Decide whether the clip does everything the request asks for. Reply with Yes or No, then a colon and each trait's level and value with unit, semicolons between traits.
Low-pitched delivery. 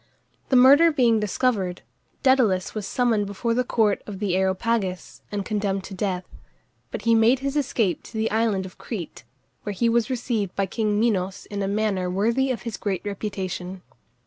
No: high, 210 Hz